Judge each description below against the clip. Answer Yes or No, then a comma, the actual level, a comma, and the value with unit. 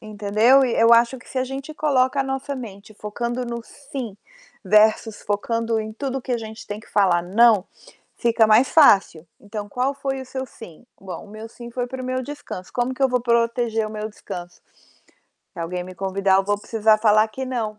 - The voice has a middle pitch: No, high, 230 Hz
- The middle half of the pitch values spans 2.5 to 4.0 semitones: Yes, average, 3.6 semitones